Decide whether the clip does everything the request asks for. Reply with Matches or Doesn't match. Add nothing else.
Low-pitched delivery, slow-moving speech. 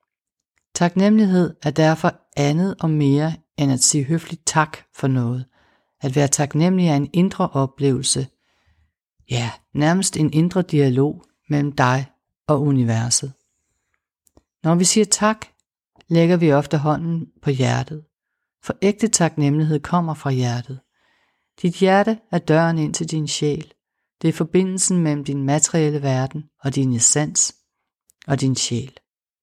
Doesn't match